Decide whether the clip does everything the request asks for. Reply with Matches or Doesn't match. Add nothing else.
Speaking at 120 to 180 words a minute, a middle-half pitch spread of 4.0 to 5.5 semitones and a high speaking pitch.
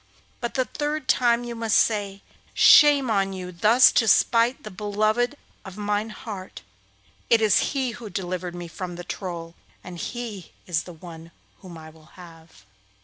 Matches